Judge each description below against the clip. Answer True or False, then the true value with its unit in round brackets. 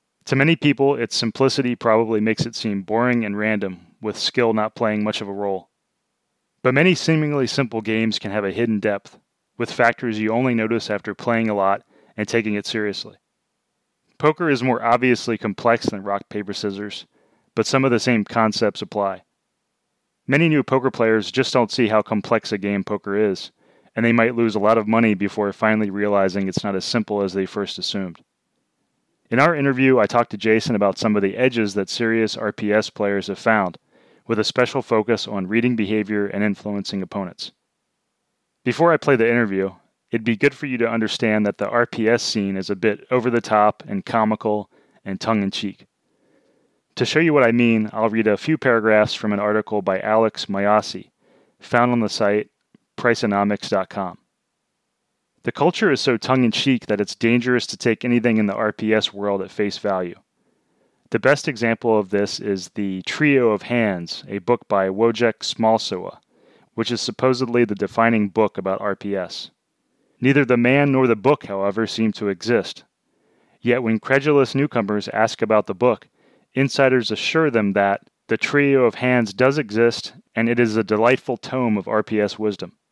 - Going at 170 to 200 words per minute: True (175 wpm)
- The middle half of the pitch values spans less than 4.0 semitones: True (2.8 semitones)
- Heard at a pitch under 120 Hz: True (110 Hz)